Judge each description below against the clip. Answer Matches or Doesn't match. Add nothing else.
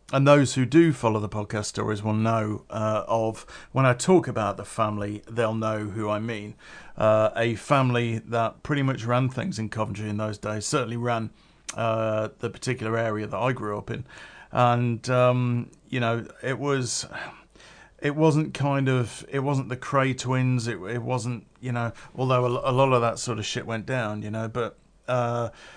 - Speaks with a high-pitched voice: Doesn't match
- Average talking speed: Matches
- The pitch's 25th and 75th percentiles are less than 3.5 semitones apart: Matches